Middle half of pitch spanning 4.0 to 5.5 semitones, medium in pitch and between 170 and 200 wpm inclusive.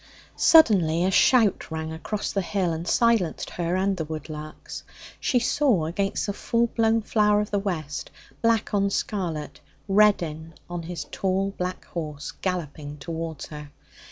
No: average, 4.6 semitones; medium, 180 Hz; average, 150 wpm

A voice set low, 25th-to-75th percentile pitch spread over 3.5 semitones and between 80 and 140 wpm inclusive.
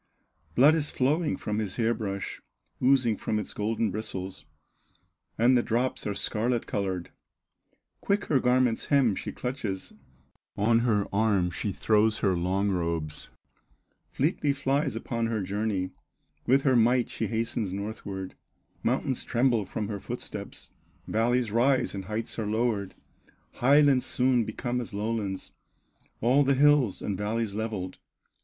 Yes: low, 115 Hz; average, 3.9 semitones; slow, 135 wpm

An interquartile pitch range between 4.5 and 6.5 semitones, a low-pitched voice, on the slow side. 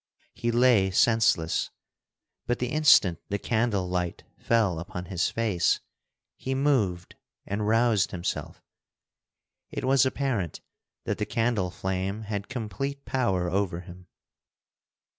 Yes: average, 5.0 semitones; low, 105 Hz; slow, 120 wpm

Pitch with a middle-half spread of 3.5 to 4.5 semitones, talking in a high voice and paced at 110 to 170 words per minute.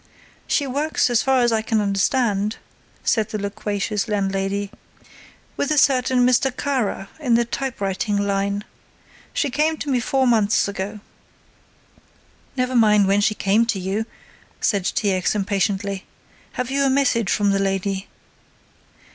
Yes: average, 4.1 semitones; high, 215 Hz; average, 145 wpm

